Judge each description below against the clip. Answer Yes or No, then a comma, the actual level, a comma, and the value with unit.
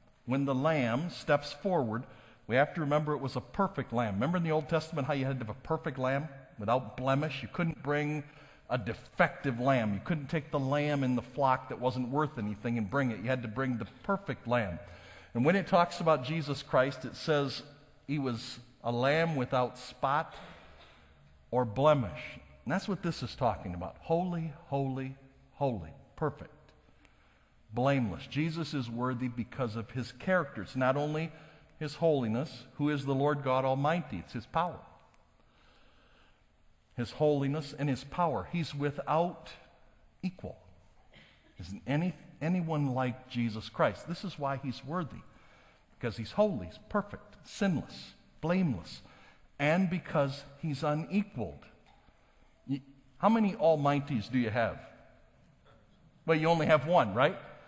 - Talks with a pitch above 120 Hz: Yes, medium, 140 Hz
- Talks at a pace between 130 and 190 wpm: Yes, average, 155 wpm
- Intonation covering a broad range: No, average, 4.3 semitones